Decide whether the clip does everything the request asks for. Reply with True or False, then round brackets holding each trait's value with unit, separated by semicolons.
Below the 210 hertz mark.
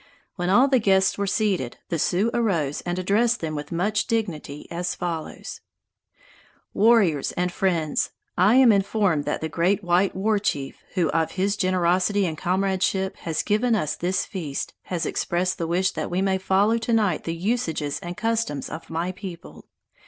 True (185 Hz)